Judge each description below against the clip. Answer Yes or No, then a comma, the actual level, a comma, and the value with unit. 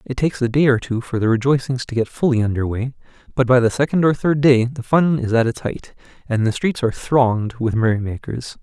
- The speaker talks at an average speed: No, fast, 235 wpm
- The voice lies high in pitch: No, low, 125 Hz